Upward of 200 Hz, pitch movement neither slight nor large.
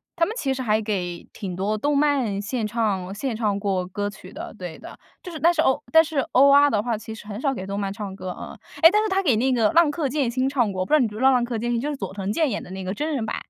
No: high, 230 Hz; wide, 5.8 semitones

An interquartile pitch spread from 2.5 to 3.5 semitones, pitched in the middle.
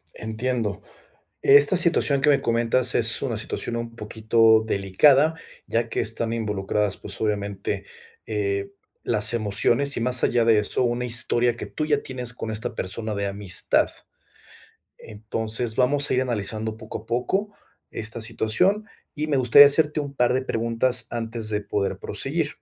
No: average, 2.9 semitones; low, 115 Hz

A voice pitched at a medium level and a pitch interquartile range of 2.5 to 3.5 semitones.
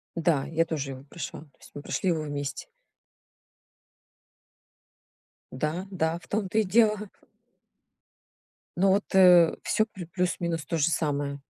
No: medium, 165 Hz; average, 4.1 semitones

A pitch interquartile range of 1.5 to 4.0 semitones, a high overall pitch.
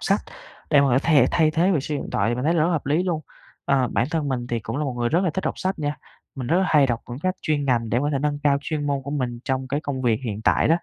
No: average, 3.6 semitones; medium, 140 Hz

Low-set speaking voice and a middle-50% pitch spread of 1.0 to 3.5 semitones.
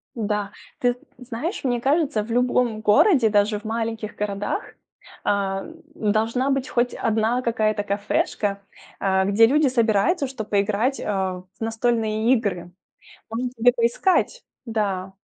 No: high, 225 Hz; average, 3.2 semitones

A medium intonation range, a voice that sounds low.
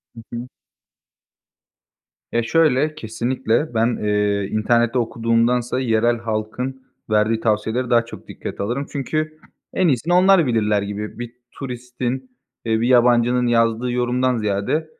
No: narrow, 2.3 semitones; low, 120 Hz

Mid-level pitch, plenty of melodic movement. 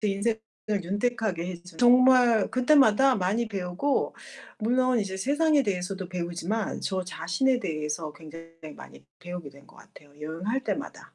No: high, 195 Hz; wide, 5.9 semitones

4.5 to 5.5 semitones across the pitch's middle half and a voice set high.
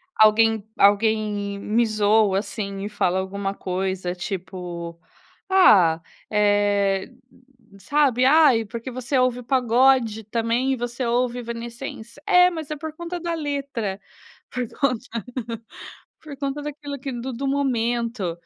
Yes: average, 4.8 semitones; high, 230 Hz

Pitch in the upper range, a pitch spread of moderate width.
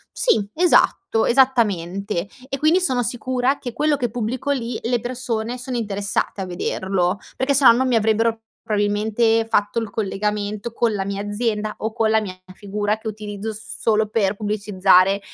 Yes: high, 220 Hz; average, 3.0 semitones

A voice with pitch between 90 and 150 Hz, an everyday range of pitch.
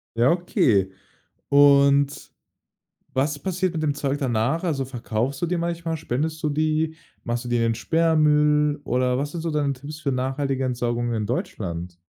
Yes: medium, 140 Hz; average, 4.1 semitones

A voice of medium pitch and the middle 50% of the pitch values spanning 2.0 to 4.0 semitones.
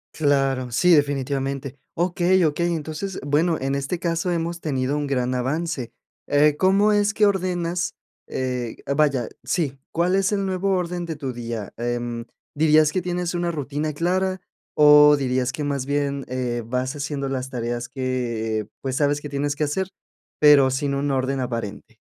No: medium, 145 Hz; average, 4.7 semitones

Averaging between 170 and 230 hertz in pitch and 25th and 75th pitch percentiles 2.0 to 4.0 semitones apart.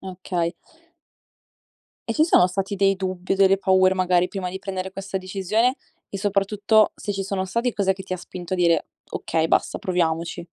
No: high, 190 Hz; narrow, 1.4 semitones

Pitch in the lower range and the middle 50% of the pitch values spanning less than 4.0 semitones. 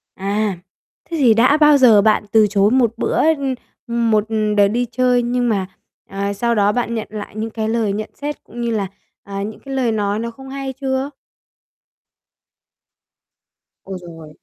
No: high, 225 Hz; average, 3.5 semitones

